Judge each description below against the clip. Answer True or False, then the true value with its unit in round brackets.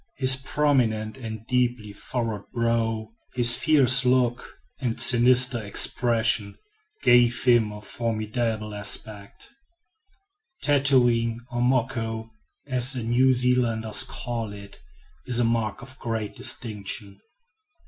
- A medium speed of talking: False (105 wpm)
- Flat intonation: True (2.3 semitones)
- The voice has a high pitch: False (120 Hz)